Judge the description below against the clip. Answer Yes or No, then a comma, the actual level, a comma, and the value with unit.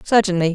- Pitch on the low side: No, high, 190 Hz